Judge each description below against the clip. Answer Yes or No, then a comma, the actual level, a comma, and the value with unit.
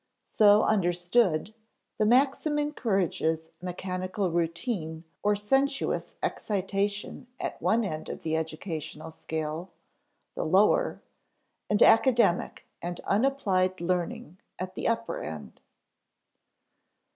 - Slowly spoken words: Yes, slow, 100 wpm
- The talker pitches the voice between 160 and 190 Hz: Yes, medium, 185 Hz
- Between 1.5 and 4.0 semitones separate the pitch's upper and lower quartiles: No, average, 4.8 semitones